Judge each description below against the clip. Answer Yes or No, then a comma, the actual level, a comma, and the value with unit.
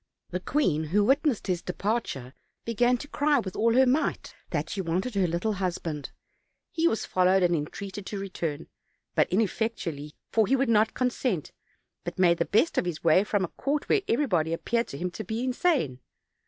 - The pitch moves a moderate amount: No, wide, 5.8 semitones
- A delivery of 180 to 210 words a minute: Yes, average, 185 wpm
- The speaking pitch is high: Yes, high, 200 Hz